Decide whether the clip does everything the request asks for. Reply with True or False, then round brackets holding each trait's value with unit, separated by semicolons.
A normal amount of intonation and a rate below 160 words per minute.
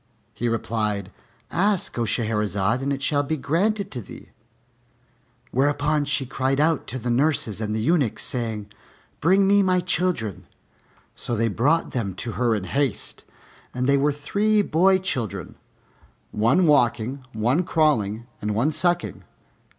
False (6.1 semitones; 145 wpm)